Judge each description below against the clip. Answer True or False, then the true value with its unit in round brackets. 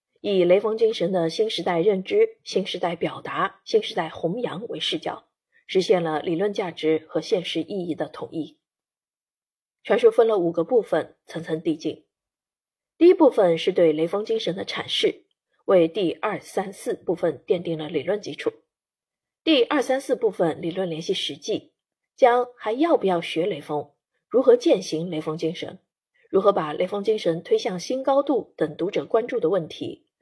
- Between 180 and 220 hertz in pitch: True (190 Hz)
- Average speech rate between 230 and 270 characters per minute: True (250 characters per minute)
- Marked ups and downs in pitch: True (7.8 semitones)